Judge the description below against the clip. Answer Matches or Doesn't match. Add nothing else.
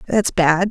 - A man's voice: Doesn't match